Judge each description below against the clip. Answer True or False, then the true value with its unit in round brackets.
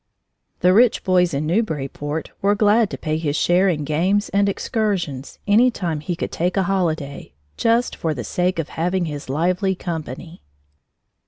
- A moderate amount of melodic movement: True (4.4 semitones)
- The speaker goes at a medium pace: True (165 wpm)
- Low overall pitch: False (175 Hz)